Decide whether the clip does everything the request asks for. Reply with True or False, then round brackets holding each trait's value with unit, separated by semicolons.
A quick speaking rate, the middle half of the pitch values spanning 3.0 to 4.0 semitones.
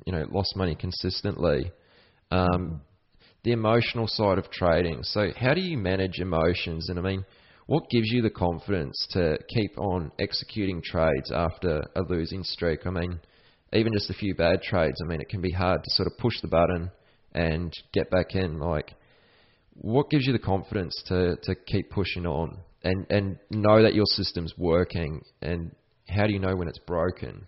True (185 wpm; 3.3 semitones)